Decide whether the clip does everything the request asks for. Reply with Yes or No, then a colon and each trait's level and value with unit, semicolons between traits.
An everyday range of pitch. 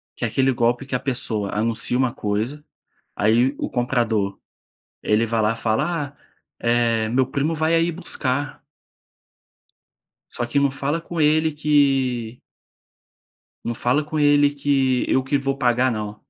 Yes: average, 3.8 semitones